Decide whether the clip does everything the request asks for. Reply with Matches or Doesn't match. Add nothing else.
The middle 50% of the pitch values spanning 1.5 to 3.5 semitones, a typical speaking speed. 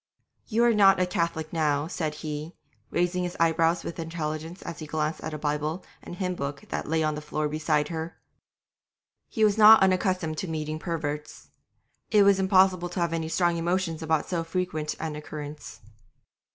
Matches